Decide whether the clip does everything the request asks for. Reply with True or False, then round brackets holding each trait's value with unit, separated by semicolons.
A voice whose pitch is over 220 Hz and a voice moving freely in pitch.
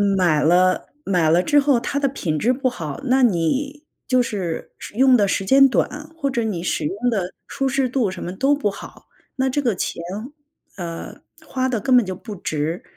True (230 Hz; 6.9 semitones)